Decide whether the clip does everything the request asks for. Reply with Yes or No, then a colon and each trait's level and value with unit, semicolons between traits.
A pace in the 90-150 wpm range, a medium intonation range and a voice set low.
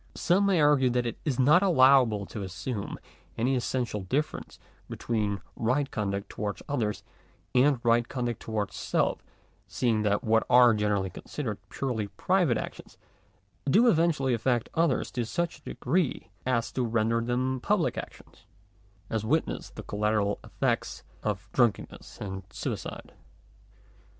Yes: average, 140 wpm; average, 4.2 semitones; low, 120 Hz